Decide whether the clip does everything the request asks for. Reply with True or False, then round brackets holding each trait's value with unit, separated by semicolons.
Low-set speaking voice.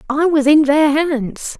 False (290 Hz)